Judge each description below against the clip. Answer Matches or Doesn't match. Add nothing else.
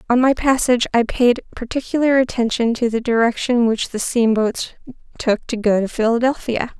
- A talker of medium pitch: Doesn't match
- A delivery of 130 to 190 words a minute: Matches